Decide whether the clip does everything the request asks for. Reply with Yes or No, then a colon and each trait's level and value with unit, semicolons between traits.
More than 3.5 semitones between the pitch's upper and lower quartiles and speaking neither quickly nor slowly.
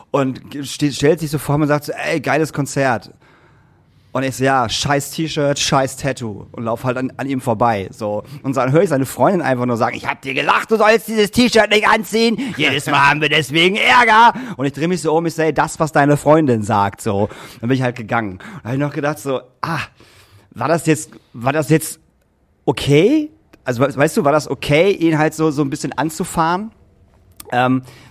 No: average, 4.3 semitones; fast, 215 wpm